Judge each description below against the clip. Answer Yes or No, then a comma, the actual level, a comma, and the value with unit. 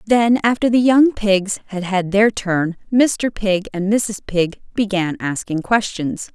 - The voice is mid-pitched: No, high, 205 Hz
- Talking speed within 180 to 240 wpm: No, average, 160 wpm